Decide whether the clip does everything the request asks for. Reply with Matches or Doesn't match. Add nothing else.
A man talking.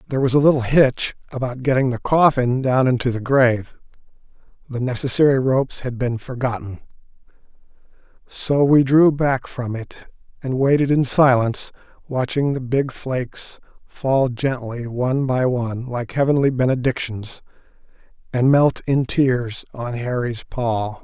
Matches